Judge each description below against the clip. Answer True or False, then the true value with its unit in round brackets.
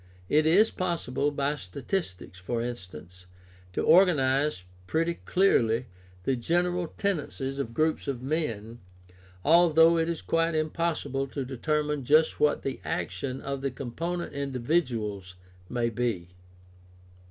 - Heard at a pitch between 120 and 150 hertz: True (140 Hz)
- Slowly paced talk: True (125 wpm)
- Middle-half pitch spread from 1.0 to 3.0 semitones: False (5.4 semitones)